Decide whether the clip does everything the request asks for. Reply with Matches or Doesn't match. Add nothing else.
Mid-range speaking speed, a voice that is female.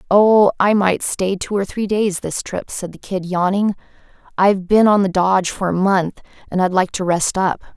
Doesn't match